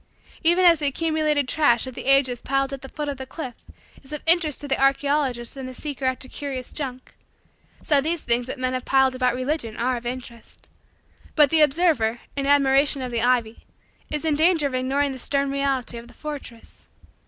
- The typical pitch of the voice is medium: No, very high, 275 Hz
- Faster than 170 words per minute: Yes, average, 200 wpm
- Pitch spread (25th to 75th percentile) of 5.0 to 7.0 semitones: No, narrow, 2.6 semitones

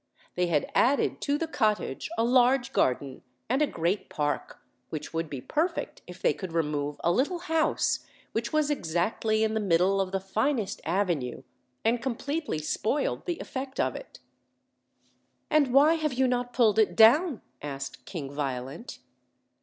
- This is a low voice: No, high, 220 Hz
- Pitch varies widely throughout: Yes, wide, 8.8 semitones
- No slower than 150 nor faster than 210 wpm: Yes, average, 160 wpm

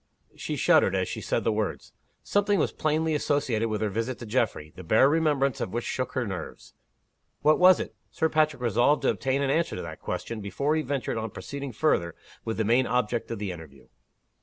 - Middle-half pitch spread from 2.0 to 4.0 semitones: No, wide, 5.4 semitones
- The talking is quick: Yes, fast, 210 wpm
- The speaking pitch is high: No, low, 125 Hz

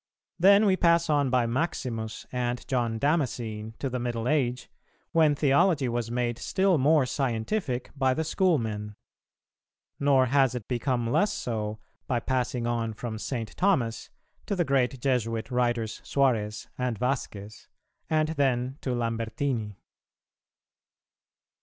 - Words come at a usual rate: No, slow, 130 wpm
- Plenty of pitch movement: No, average, 3.6 semitones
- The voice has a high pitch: No, low, 125 Hz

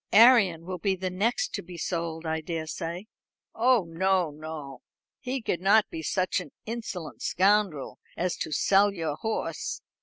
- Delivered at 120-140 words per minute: No, average, 155 wpm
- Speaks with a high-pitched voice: No, medium, 180 Hz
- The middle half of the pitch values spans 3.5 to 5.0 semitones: Yes, average, 4.0 semitones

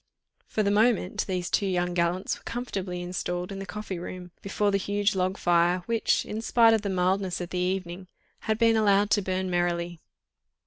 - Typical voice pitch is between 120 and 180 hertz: No, high, 190 Hz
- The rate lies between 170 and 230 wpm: Yes, average, 190 wpm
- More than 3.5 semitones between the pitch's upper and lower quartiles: No, narrow, 2.5 semitones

